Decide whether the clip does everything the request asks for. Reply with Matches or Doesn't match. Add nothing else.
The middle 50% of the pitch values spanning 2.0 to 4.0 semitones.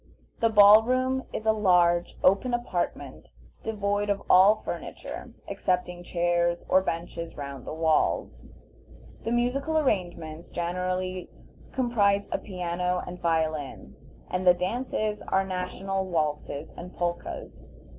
Matches